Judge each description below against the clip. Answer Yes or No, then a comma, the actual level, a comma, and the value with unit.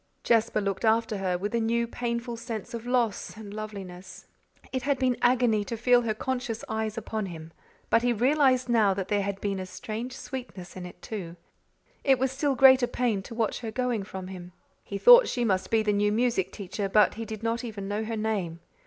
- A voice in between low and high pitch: No, high, 220 Hz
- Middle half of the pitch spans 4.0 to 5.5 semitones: No, average, 3.4 semitones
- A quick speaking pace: Yes, fast, 210 wpm